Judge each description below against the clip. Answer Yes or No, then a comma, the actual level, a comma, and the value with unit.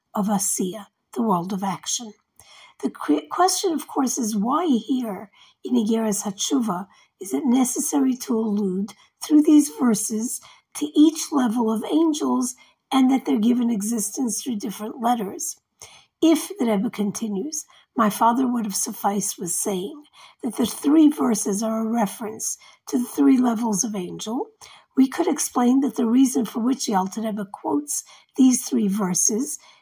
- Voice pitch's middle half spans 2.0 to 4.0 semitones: No, average, 4.4 semitones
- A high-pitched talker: Yes, high, 235 Hz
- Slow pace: No, average, 150 wpm